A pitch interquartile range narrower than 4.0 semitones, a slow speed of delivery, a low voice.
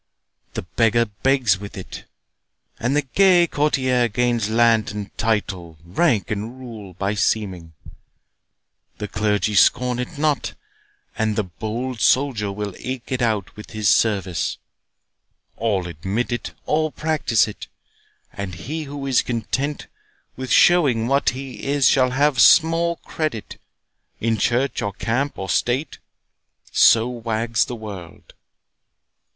No: average, 4.4 semitones; slow, 125 wpm; low, 115 Hz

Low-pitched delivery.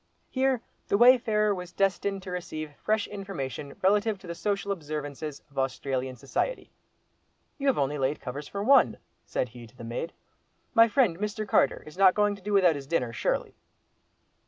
No: medium, 185 Hz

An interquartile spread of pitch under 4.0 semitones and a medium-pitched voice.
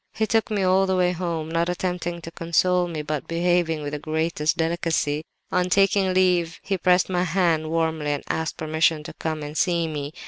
Yes: narrow, 2.4 semitones; medium, 170 Hz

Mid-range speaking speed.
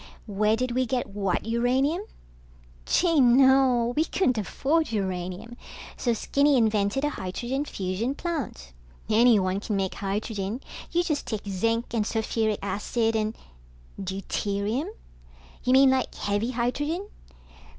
No: slow, 125 wpm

